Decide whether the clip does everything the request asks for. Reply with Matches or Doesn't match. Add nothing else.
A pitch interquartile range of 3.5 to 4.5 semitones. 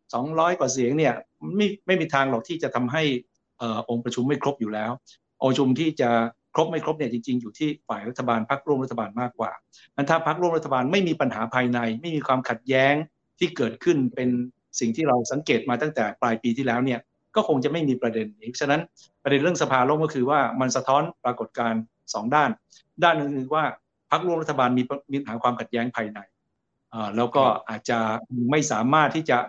Matches